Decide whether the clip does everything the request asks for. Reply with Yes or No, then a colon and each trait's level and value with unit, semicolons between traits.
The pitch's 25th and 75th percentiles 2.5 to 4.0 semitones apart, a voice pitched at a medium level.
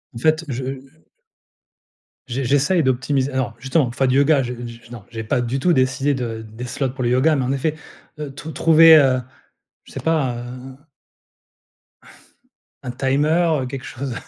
No: average, 2.9 semitones; low, 130 Hz